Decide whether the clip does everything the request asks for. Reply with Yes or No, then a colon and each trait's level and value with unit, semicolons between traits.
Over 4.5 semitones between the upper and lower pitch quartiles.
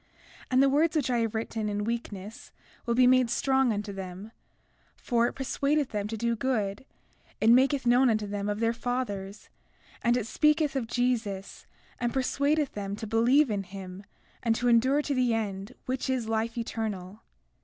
No: average, 3.7 semitones